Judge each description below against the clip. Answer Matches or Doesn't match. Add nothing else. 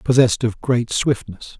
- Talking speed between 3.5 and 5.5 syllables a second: Matches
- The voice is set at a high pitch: Doesn't match